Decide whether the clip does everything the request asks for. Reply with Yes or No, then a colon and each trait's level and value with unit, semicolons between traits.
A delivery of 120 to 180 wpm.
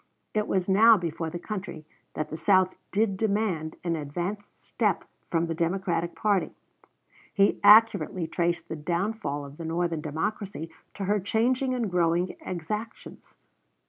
Yes: average, 145 wpm